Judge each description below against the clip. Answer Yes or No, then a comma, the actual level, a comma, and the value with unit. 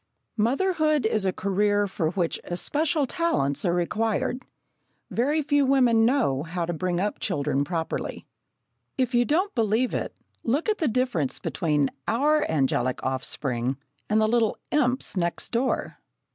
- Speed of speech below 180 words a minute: Yes, average, 145 wpm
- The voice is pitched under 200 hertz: No, high, 220 Hz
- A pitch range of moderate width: No, wide, 7.7 semitones